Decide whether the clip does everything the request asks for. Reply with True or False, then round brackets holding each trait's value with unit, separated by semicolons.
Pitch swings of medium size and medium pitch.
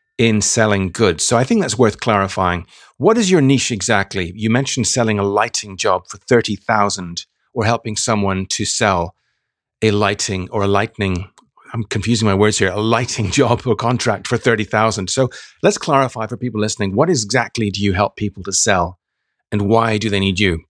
False (3.0 semitones; 105 Hz)